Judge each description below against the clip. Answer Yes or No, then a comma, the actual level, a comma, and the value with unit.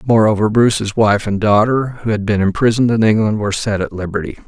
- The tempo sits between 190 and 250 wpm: Yes, average, 200 wpm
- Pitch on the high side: No, low, 105 Hz